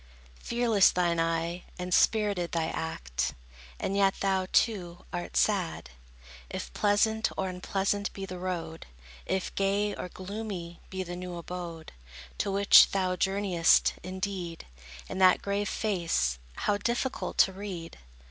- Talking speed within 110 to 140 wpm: Yes, slow, 135 wpm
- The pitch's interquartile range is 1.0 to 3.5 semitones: Yes, average, 2.7 semitones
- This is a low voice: No, medium, 185 Hz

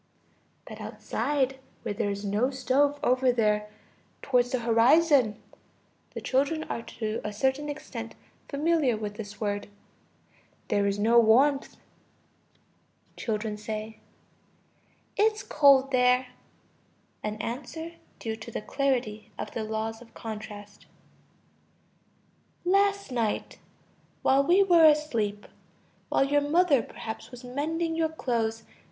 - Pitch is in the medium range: No, very high, 250 Hz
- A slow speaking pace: Yes, slow, 115 wpm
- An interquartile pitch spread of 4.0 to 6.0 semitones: Yes, average, 5.0 semitones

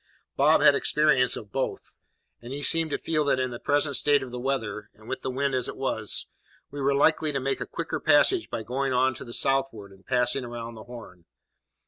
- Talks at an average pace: No, fast, 220 wpm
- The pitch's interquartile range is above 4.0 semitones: No, average, 2.9 semitones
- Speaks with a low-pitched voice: Yes, low, 130 Hz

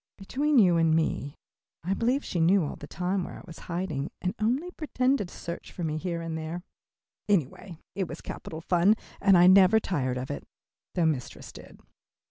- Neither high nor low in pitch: Yes, medium, 175 Hz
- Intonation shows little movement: No, average, 3.8 semitones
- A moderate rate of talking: Yes, average, 190 wpm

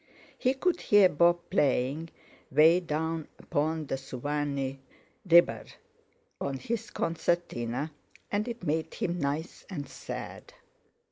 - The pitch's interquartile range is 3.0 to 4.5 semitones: Yes, average, 3.6 semitones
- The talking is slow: Yes, slow, 115 wpm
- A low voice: No, medium, 160 Hz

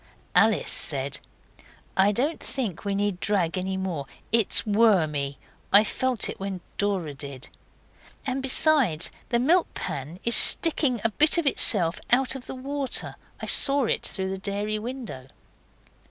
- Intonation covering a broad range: Yes, wide, 6.1 semitones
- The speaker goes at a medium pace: Yes, average, 155 wpm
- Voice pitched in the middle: No, high, 205 Hz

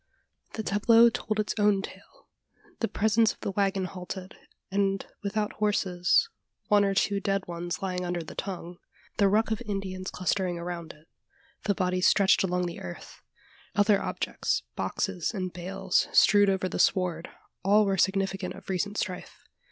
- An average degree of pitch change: No, narrow, 2.1 semitones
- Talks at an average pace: Yes, average, 160 wpm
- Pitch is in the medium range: No, high, 195 Hz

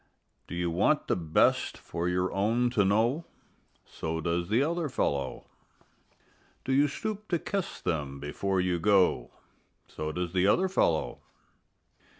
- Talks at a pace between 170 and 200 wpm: No, average, 145 wpm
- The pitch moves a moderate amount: No, wide, 7.7 semitones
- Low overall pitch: Yes, very low, 95 Hz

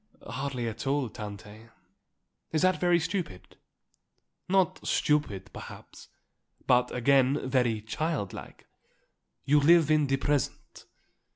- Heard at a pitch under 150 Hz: Yes, low, 135 Hz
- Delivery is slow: Yes, slow, 110 wpm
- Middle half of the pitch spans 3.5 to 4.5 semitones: No, average, 5.1 semitones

